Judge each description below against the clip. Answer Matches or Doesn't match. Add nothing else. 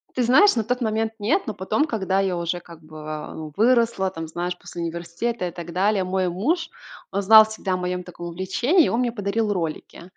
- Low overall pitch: Doesn't match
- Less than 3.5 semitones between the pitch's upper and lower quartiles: Doesn't match